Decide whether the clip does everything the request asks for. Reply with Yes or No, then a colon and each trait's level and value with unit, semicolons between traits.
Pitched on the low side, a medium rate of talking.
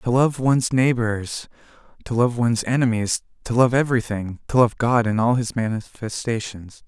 Yes: low, 115 Hz; average, 155 wpm